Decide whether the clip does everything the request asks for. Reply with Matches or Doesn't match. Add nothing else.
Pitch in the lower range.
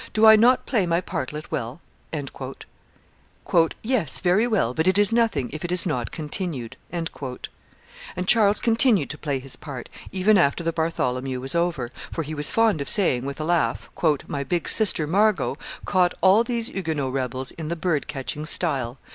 Doesn't match